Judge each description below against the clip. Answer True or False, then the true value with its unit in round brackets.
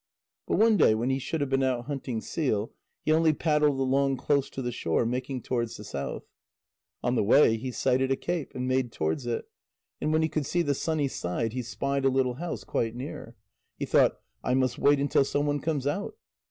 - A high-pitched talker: False (135 Hz)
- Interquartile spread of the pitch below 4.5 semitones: True (3.0 semitones)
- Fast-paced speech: True (215 wpm)